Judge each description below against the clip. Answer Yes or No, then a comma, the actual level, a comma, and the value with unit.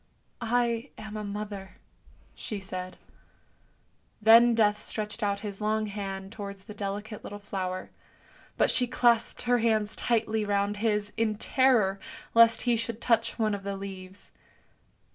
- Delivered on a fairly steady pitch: Yes, narrow, 2.3 semitones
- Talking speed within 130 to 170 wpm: Yes, average, 145 wpm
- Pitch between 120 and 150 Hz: No, high, 210 Hz